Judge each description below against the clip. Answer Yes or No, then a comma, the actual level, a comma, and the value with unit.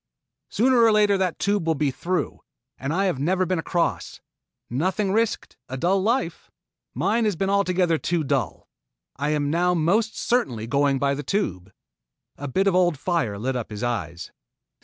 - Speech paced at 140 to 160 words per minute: No, average, 180 wpm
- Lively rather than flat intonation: Yes, wide, 6.0 semitones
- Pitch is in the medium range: Yes, medium, 175 Hz